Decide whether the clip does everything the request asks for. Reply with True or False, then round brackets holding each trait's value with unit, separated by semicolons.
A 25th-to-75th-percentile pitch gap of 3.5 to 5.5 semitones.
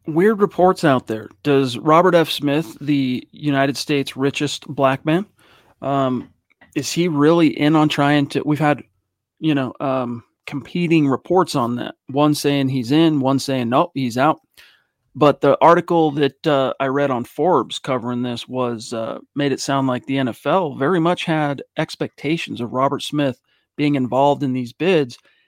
False (3.0 semitones)